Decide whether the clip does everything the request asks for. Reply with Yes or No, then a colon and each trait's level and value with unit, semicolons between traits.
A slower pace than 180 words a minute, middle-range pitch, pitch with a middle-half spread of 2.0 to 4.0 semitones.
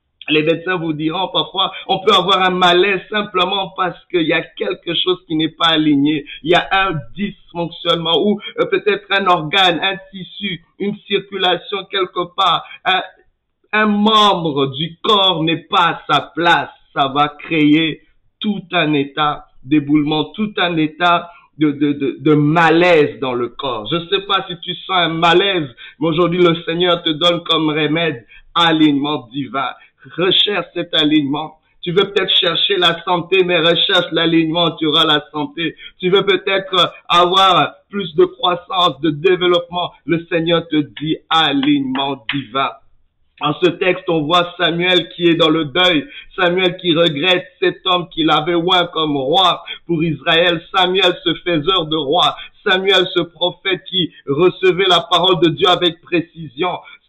Yes: average, 160 wpm; medium, 170 Hz; average, 2.7 semitones